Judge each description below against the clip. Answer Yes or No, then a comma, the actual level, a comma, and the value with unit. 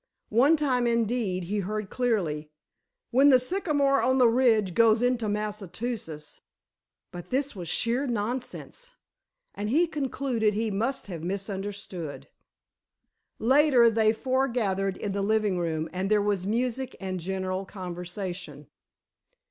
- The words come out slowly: Yes, slow, 130 wpm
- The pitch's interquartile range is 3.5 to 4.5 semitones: No, average, 4.9 semitones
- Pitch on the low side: No, high, 215 Hz